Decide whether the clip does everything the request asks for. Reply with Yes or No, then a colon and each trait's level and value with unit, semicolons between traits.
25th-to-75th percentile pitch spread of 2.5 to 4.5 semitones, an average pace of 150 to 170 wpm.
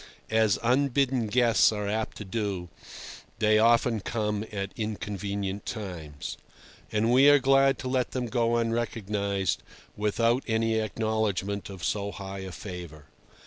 No: average, 2.8 semitones; slow, 135 wpm